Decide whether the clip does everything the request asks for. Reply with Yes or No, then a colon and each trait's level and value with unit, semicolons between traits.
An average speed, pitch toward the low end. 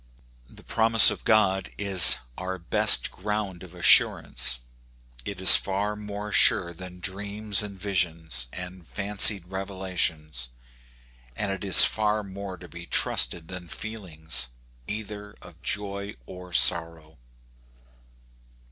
No: slow, 120 wpm; very low, 95 Hz